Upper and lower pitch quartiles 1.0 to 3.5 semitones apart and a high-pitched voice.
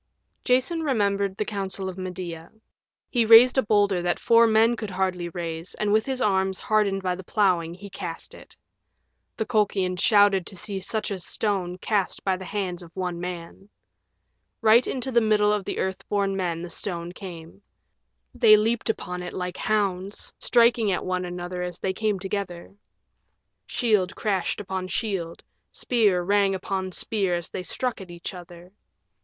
Yes: average, 2.9 semitones; high, 195 Hz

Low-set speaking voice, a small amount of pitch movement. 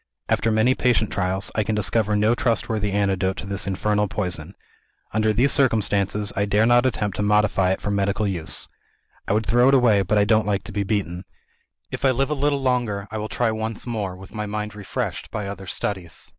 Yes: low, 105 Hz; narrow, 2.1 semitones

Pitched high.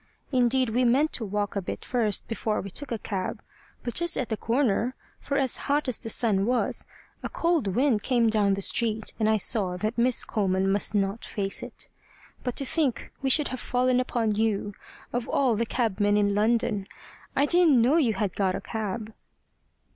Yes: high, 225 Hz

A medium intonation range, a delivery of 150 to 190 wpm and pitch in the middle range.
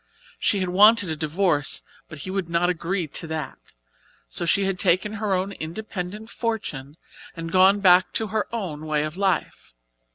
Yes: average, 3.7 semitones; average, 170 wpm; medium, 180 Hz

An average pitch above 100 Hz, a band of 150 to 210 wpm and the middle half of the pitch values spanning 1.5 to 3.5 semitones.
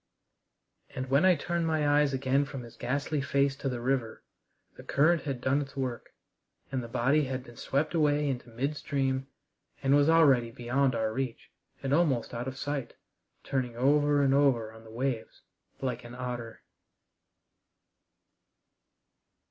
Yes: low, 135 Hz; average, 155 wpm; average, 2.7 semitones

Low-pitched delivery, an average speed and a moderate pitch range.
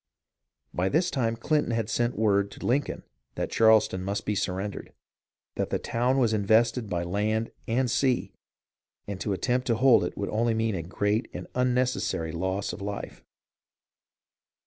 Yes: low, 110 Hz; average, 160 wpm; average, 3.5 semitones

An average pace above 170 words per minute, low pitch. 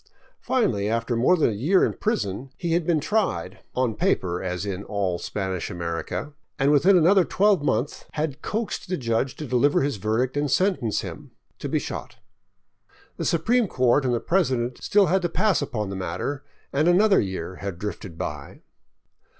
Yes: average, 185 wpm; low, 130 Hz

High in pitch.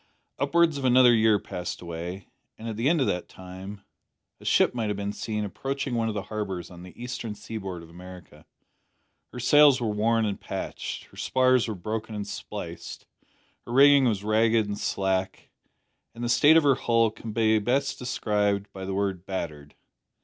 No: low, 110 Hz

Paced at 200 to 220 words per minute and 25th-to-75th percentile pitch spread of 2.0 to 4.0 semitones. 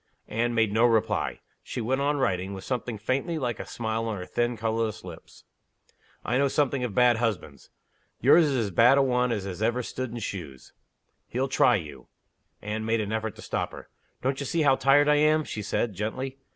Yes: fast, 205 wpm; average, 3.6 semitones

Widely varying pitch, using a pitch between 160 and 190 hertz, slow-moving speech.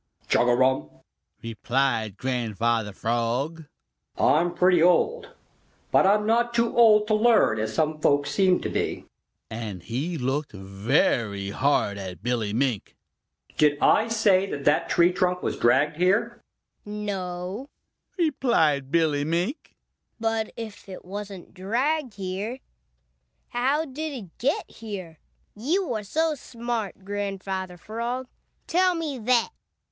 Yes: wide, 9.0 semitones; medium, 185 Hz; slow, 125 wpm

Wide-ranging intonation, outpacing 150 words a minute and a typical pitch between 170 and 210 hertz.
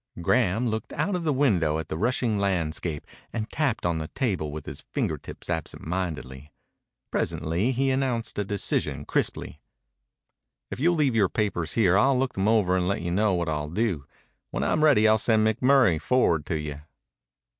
No: wide, 7.0 semitones; average, 175 wpm; low, 100 Hz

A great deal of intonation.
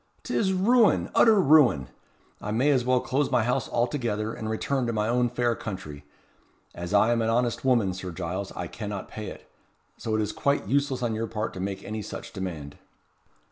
No: average, 4.2 semitones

